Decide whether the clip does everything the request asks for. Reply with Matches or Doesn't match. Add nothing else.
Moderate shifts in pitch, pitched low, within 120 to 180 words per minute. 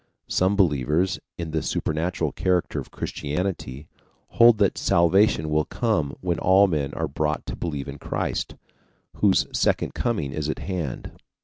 Matches